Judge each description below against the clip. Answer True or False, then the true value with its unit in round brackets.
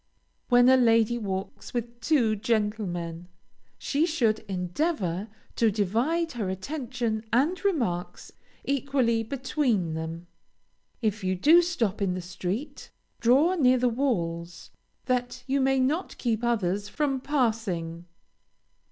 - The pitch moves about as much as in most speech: False (5.9 semitones)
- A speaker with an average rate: False (120 wpm)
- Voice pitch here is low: False (230 Hz)